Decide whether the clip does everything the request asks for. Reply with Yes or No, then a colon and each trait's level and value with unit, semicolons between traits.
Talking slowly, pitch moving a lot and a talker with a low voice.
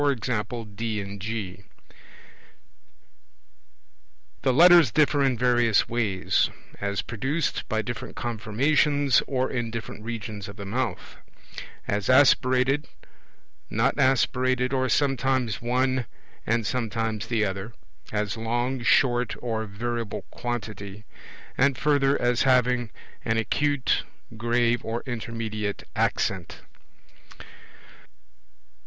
No: slow, 100 wpm; average, 3.0 semitones; low, 120 Hz